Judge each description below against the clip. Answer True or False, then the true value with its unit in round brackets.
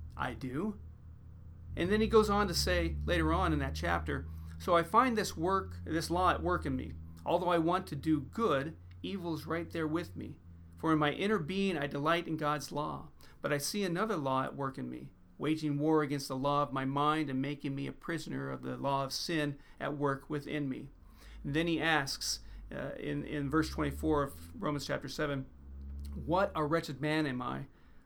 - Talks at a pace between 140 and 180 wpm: False (205 wpm)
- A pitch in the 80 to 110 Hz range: False (140 Hz)